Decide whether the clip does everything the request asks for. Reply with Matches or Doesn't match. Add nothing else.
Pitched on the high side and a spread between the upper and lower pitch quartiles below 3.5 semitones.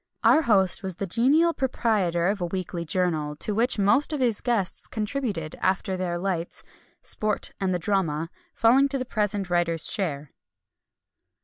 Doesn't match